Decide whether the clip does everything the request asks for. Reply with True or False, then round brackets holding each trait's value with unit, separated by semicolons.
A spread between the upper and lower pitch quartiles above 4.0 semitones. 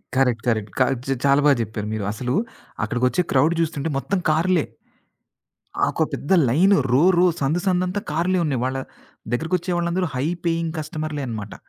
True (5.4 semitones)